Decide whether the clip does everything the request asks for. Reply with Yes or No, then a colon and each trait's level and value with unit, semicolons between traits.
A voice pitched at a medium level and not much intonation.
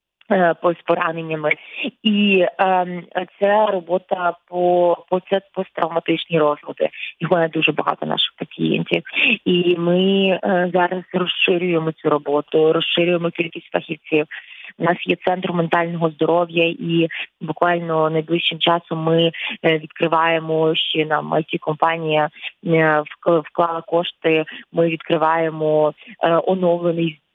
Yes: medium, 170 Hz; narrow, 1.8 semitones